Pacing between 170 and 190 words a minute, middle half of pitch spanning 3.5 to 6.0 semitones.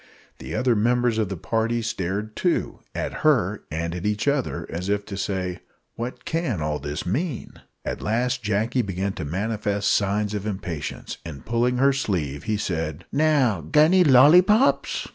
No: average, 160 wpm; average, 5.3 semitones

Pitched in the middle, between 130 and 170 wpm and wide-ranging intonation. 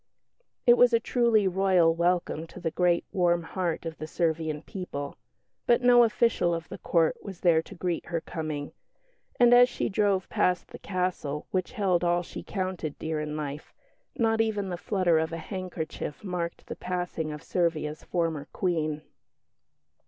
No: medium, 175 Hz; average, 165 wpm; average, 3.1 semitones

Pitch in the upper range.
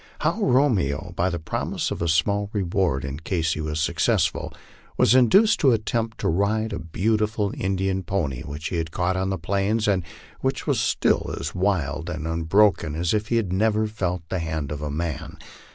No: very low, 95 Hz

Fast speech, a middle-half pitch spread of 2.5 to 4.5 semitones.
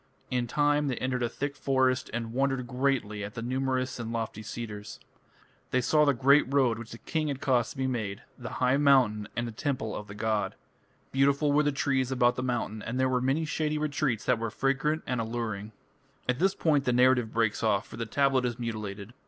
Yes: fast, 210 wpm; average, 3.2 semitones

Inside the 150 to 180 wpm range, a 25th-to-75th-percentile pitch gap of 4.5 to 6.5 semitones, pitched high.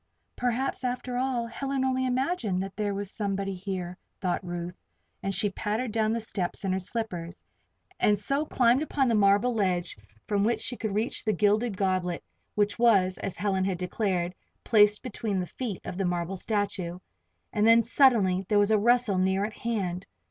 No: average, 175 wpm; average, 3.8 semitones; high, 205 Hz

